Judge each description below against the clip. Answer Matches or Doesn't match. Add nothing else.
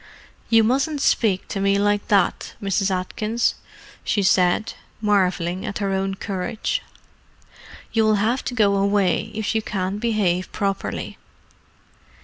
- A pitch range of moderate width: Doesn't match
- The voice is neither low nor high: Doesn't match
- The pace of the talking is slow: Matches